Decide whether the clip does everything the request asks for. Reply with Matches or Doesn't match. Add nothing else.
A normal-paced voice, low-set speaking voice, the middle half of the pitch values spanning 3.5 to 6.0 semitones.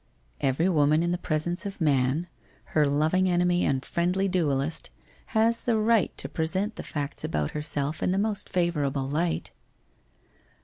Doesn't match